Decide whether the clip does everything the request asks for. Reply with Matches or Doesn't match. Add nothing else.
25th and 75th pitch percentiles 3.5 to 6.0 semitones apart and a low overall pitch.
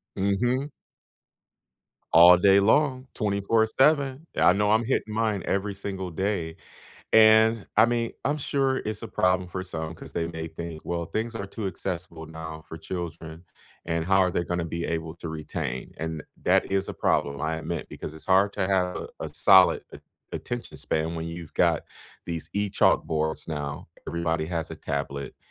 Matches